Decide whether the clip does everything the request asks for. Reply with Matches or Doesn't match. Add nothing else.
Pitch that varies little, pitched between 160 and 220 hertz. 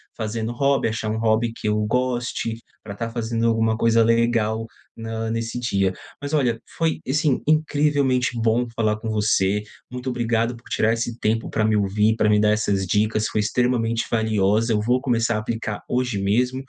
Doesn't match